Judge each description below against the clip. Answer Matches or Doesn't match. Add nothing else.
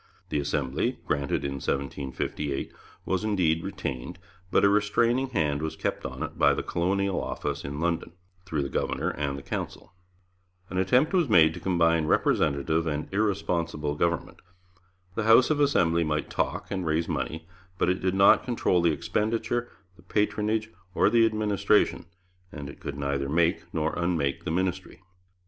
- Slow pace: Doesn't match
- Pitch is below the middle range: Matches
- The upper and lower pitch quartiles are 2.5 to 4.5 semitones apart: Doesn't match